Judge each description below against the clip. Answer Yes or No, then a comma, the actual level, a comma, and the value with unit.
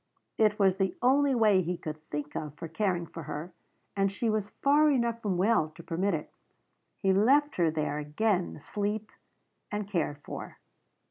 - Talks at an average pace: Yes, average, 175 wpm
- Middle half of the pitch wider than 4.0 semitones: Yes, average, 4.8 semitones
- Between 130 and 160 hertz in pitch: No, high, 195 Hz